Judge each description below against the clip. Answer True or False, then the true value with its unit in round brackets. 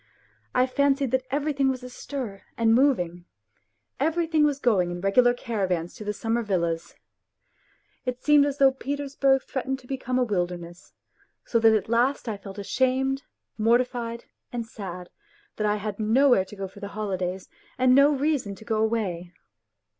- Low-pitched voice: False (235 Hz)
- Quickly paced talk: False (160 wpm)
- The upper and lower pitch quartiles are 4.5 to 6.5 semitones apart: True (5.1 semitones)